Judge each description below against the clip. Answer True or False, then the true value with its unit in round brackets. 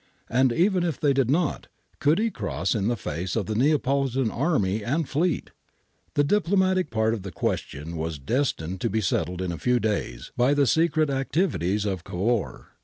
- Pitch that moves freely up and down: True (7.5 semitones)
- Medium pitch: False (120 Hz)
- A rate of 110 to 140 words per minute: False (180 wpm)